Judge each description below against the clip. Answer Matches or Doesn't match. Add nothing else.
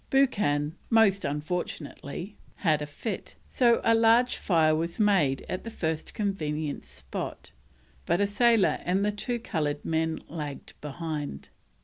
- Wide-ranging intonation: Matches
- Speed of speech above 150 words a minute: Doesn't match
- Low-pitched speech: Doesn't match